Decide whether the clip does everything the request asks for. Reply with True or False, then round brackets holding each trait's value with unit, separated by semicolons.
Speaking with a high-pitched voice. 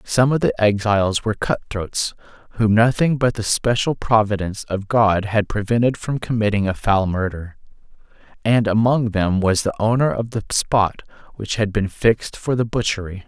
False (105 Hz)